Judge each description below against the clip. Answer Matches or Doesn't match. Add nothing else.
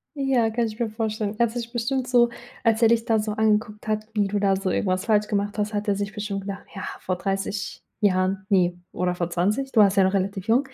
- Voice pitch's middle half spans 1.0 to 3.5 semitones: Matches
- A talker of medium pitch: Doesn't match